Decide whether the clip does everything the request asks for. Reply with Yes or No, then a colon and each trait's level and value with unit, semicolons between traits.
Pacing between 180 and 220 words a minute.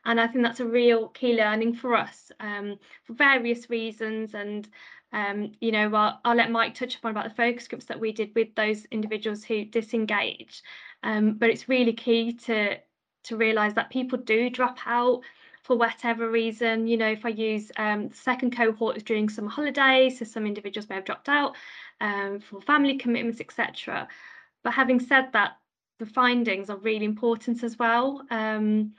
Yes: average, 185 wpm